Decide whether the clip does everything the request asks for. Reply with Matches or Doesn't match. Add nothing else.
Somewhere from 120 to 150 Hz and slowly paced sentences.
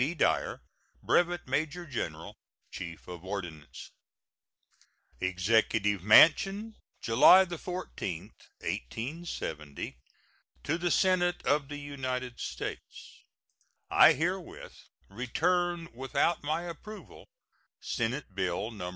Matches